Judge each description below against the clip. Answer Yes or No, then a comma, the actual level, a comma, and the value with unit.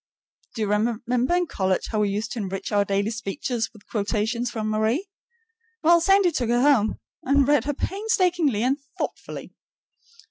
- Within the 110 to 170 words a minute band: Yes, average, 165 wpm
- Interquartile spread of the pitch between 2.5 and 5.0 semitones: No, wide, 5.4 semitones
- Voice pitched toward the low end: No, high, 235 Hz